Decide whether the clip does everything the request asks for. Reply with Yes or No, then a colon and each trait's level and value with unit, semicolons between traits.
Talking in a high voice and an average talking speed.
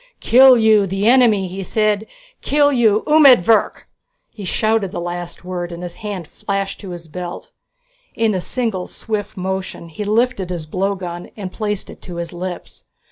Yes: high, 195 Hz; average, 165 wpm